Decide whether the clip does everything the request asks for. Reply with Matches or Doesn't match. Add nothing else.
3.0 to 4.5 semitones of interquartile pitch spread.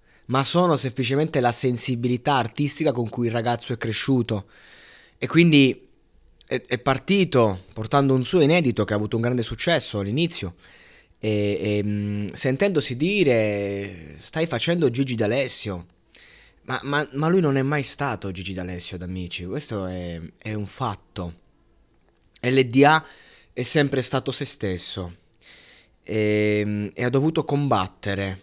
Doesn't match